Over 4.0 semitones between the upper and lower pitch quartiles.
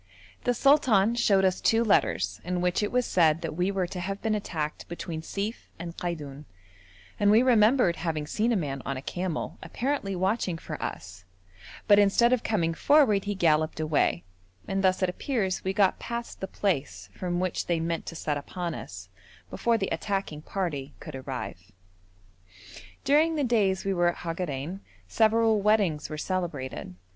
Yes: average, 5.0 semitones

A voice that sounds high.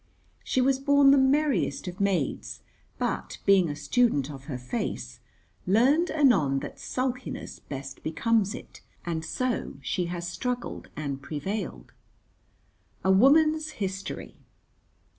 Yes: high, 195 Hz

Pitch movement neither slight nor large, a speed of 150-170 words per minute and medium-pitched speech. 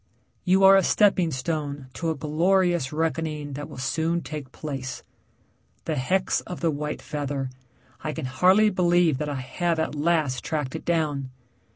Yes: average, 3.4 semitones; average, 165 wpm; medium, 155 Hz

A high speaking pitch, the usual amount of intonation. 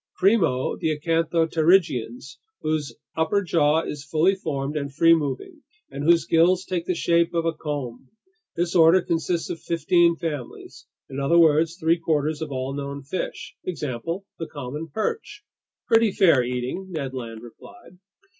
No: medium, 160 Hz; average, 3.3 semitones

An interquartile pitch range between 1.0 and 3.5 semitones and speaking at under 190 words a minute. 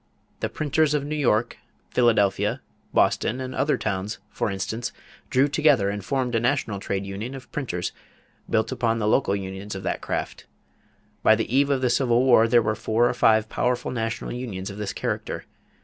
No: average, 4.2 semitones; average, 180 wpm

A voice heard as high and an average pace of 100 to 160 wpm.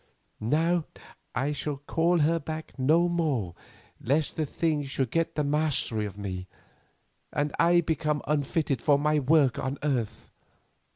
No: medium, 150 Hz; average, 140 wpm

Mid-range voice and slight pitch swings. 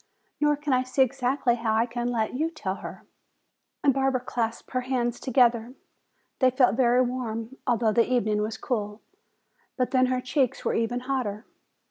No: high, 245 Hz; narrow, 2.2 semitones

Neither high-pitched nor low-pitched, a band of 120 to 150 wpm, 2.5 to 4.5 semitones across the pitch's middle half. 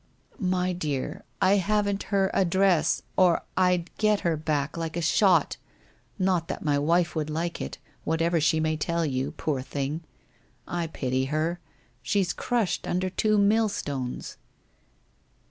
Yes: medium, 170 Hz; average, 145 wpm; average, 3.6 semitones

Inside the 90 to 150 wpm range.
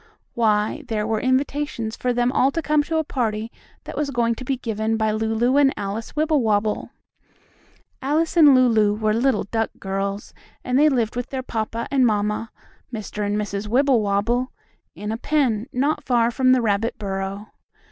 No: average, 170 wpm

